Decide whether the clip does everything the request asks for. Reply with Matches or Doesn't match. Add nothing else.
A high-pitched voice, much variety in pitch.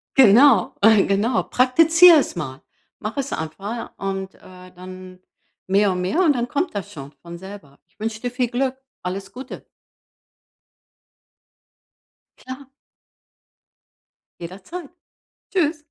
Matches